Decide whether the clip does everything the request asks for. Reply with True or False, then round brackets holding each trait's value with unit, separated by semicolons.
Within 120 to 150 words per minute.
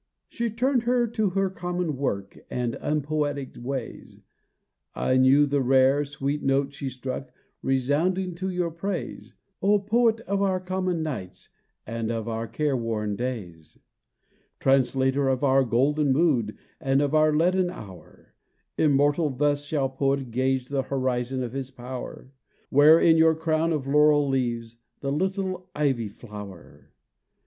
True (140 wpm)